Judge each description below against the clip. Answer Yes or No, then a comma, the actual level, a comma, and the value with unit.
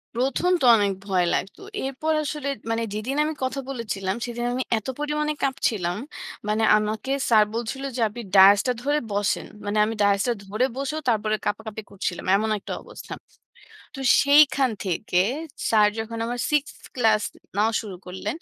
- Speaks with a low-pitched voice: No, high, 225 Hz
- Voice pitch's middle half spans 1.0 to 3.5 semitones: No, average, 4.6 semitones